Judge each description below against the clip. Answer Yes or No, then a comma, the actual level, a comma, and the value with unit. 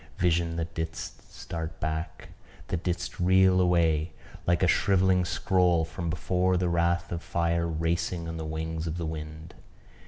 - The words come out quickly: No, average, 155 wpm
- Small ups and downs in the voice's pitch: Yes, narrow, 1.5 semitones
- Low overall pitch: Yes, very low, 85 Hz